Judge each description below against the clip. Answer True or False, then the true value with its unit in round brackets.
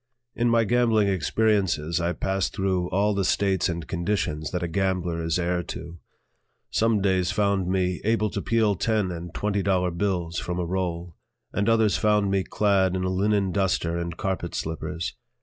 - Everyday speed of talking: True (175 wpm)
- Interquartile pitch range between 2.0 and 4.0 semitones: True (2.9 semitones)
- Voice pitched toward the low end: True (95 Hz)